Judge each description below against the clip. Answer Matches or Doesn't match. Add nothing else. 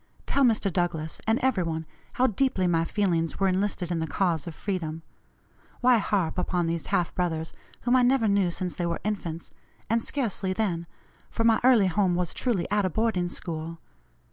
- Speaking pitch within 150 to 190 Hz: Matches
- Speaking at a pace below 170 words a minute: Doesn't match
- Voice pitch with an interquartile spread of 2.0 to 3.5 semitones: Doesn't match